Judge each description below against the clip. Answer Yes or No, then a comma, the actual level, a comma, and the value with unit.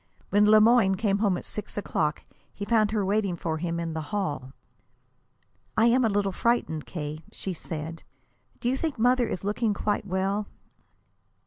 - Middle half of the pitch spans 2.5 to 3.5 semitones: No, average, 4.4 semitones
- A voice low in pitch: No, high, 200 Hz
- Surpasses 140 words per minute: Yes, average, 180 wpm